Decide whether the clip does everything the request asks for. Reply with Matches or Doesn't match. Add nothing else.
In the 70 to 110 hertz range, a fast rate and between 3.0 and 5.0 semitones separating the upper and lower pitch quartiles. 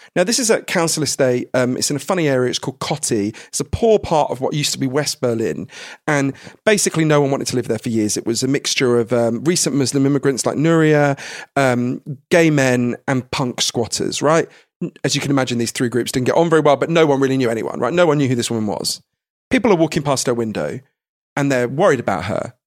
Doesn't match